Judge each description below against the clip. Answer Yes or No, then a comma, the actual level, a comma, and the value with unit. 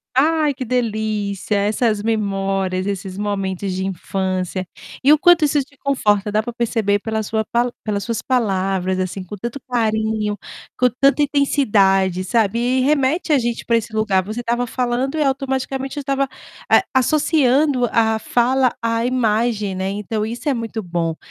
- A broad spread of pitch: No, average, 4.5 semitones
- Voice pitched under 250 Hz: Yes, high, 225 Hz